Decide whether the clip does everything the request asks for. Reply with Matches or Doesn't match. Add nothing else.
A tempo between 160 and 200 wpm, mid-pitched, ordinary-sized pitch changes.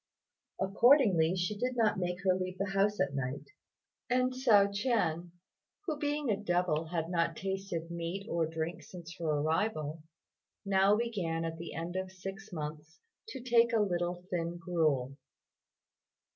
Doesn't match